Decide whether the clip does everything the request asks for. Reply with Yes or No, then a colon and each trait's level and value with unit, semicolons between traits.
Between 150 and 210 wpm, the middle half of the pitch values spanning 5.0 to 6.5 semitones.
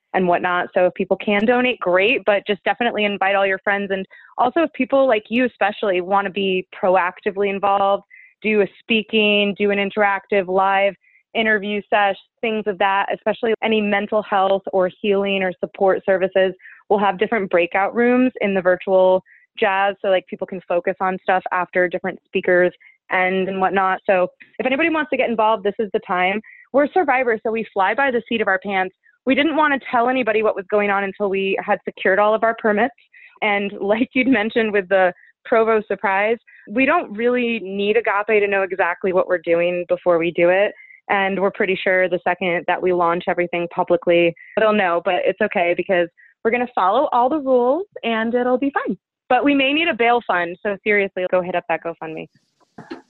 No: average, 200 wpm; average, 3.1 semitones